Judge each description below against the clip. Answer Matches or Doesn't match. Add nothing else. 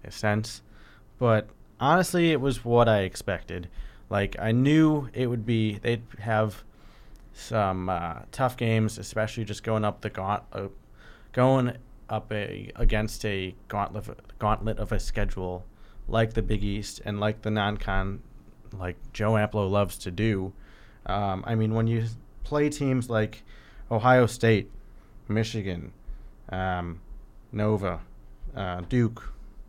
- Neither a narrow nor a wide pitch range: Doesn't match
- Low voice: Matches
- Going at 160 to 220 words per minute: Doesn't match